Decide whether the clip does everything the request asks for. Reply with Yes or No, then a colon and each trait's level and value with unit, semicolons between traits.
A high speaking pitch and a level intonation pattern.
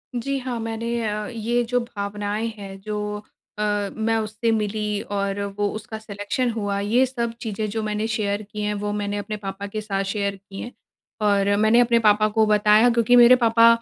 Yes: high, 215 Hz; narrow, 2.1 semitones